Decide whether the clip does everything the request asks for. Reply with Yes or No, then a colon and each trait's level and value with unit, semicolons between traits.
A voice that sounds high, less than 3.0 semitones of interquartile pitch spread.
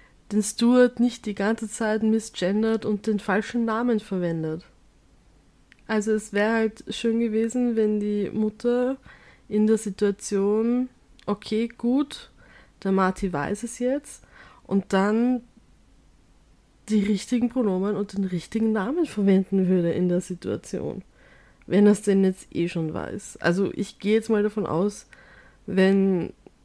Yes: high, 210 Hz; narrow, 2.5 semitones